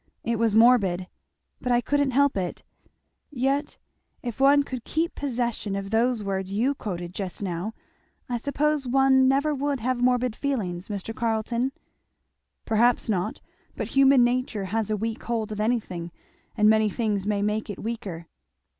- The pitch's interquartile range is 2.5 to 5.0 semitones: Yes, average, 4.0 semitones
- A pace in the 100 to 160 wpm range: Yes, average, 155 wpm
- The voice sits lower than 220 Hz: No, high, 230 Hz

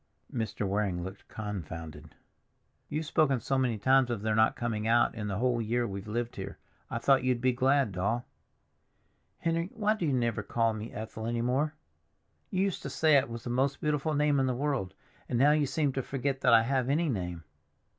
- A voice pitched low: Yes, low, 120 Hz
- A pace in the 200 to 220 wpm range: Yes, fast, 205 wpm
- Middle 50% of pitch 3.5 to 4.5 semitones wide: Yes, average, 4.2 semitones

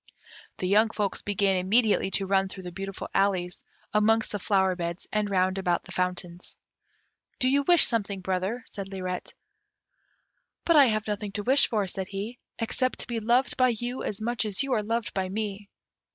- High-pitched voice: Yes, high, 205 Hz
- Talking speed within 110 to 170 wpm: No, average, 185 wpm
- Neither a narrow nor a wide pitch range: Yes, average, 3.2 semitones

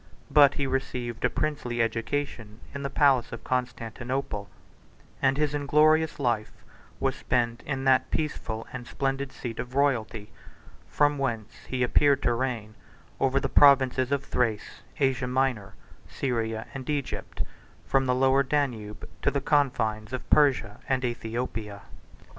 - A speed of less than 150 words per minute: Yes, average, 140 wpm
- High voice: No, low, 130 Hz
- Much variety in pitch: No, average, 3.1 semitones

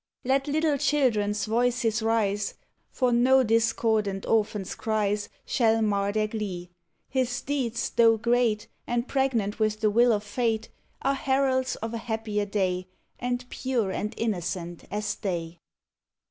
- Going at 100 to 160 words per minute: Yes, slow, 135 wpm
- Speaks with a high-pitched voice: Yes, high, 225 Hz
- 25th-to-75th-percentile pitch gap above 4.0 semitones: No, average, 3.0 semitones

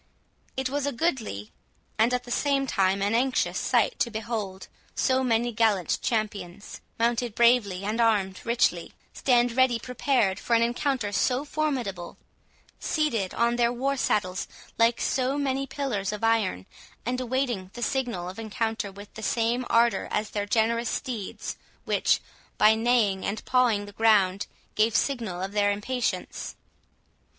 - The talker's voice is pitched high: Yes, high, 230 Hz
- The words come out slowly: No, average, 150 wpm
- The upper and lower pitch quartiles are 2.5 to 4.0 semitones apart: Yes, average, 3.6 semitones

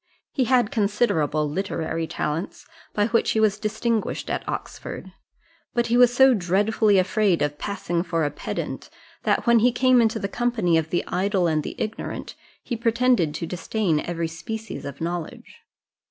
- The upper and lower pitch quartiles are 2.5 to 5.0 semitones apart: No, wide, 5.5 semitones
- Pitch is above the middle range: Yes, high, 200 Hz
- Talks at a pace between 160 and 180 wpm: Yes, average, 165 wpm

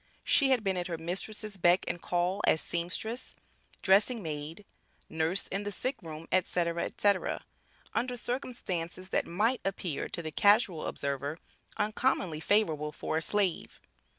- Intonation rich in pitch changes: No, average, 4.2 semitones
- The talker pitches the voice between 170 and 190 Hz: Yes, medium, 185 Hz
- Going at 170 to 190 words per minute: No, average, 140 wpm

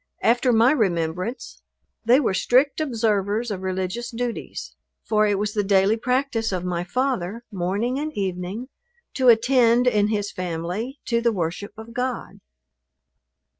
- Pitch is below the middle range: No, high, 220 Hz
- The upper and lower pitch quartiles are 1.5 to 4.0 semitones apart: No, average, 4.4 semitones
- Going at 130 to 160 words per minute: Yes, average, 140 wpm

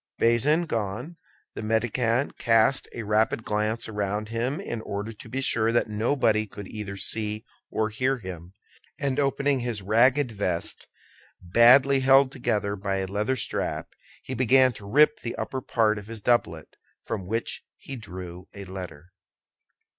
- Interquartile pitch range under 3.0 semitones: No, average, 4.0 semitones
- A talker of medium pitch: No, low, 110 Hz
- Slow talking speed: No, average, 155 wpm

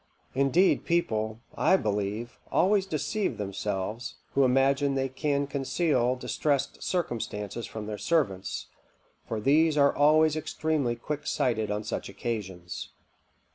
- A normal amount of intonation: No, wide, 5.9 semitones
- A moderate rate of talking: No, slow, 115 wpm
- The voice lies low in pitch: Yes, low, 130 Hz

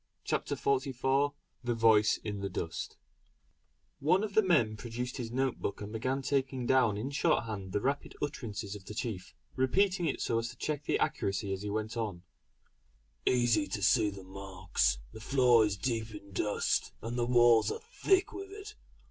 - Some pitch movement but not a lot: Yes, average, 4.6 semitones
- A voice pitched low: Yes, low, 120 Hz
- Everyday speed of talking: Yes, average, 180 wpm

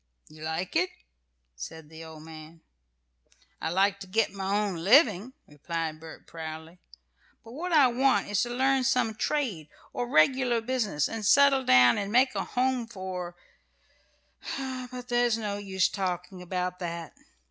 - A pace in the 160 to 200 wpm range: No, average, 150 wpm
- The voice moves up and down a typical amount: No, wide, 6.9 semitones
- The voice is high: Yes, high, 200 Hz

